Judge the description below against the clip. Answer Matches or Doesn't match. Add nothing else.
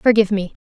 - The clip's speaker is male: Doesn't match